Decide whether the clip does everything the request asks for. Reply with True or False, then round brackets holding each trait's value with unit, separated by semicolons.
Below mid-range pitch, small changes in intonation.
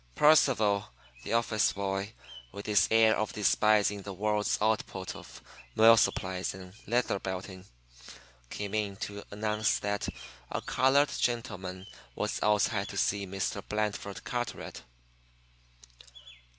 True (105 Hz; 1.8 semitones)